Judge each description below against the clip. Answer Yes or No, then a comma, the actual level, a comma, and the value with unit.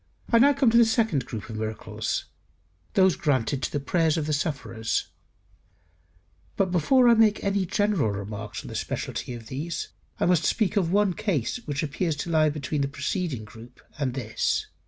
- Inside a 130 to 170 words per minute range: No, average, 180 wpm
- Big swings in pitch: Yes, wide, 7.1 semitones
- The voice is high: No, medium, 155 Hz